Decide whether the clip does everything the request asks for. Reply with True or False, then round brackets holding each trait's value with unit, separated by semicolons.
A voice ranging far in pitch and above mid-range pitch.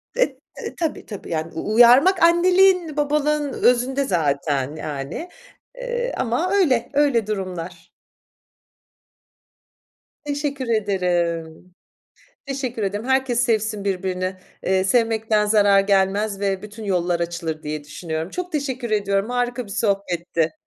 True (6.7 semitones; 210 Hz)